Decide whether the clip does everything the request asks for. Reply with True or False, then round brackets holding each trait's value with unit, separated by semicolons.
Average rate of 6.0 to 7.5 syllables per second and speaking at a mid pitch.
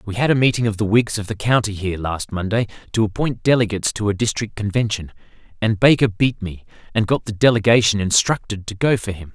False (6.1 syllables/s; 105 Hz)